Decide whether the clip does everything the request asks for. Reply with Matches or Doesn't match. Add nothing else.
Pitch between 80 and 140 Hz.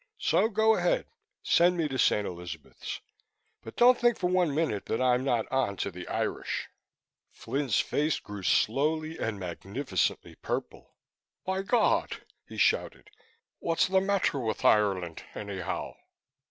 Matches